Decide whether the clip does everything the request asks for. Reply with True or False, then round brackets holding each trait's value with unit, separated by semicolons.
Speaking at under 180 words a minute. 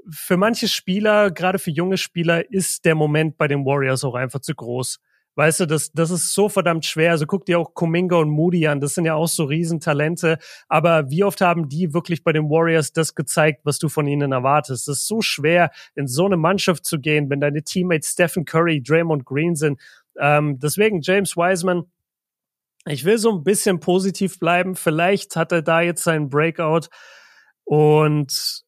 False (190 wpm)